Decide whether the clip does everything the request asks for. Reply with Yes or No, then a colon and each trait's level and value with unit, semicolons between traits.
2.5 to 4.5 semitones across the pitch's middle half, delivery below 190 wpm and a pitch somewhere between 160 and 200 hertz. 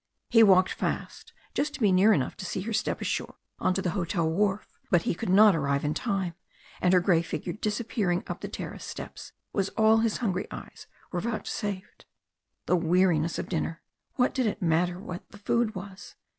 No: average, 3.4 semitones; average, 195 wpm; high, 190 Hz